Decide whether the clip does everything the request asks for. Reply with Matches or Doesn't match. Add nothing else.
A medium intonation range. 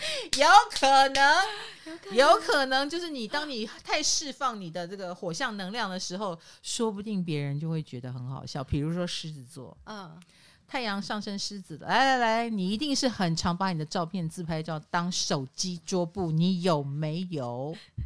Doesn't match